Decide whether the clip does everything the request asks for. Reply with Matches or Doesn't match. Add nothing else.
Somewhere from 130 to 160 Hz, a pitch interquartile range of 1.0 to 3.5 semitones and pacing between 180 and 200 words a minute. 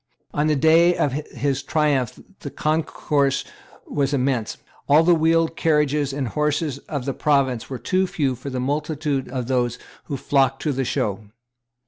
Doesn't match